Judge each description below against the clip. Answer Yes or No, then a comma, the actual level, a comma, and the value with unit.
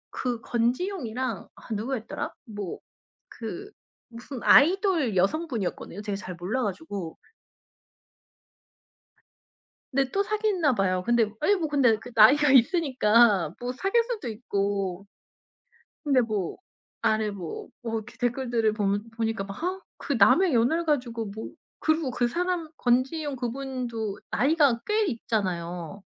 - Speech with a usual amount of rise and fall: No, wide, 5.8 semitones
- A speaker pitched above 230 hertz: Yes, high, 240 Hz